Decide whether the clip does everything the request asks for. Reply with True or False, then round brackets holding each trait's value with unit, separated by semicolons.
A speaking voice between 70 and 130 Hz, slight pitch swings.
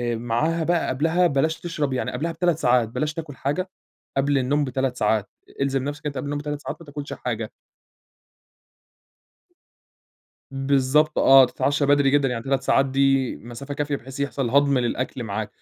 False (140 Hz; 2.2 semitones)